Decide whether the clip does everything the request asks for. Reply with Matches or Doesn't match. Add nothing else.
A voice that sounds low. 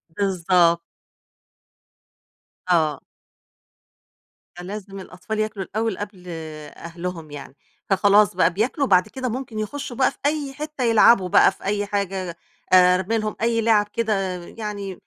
Doesn't match